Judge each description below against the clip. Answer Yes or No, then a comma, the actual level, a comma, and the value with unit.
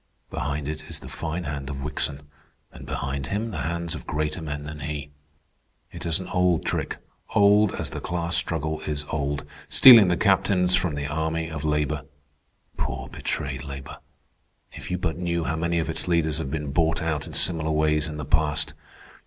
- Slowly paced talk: No, average, 185 wpm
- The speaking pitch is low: Yes, very low, 80 Hz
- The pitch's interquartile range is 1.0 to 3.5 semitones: Yes, narrow, 2.5 semitones